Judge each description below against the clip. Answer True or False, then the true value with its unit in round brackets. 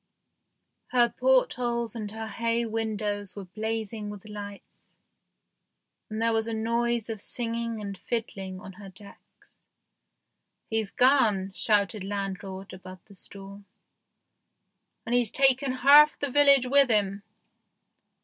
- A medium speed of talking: False (125 wpm)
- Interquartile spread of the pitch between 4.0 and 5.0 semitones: False (2.9 semitones)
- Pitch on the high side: True (220 Hz)